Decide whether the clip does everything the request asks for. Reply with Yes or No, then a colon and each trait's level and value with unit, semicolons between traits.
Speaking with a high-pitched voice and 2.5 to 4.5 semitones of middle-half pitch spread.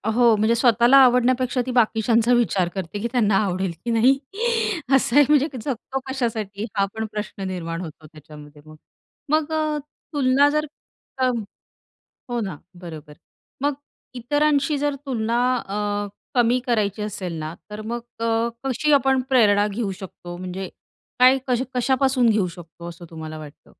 No: high, 230 Hz; average, 5.1 semitones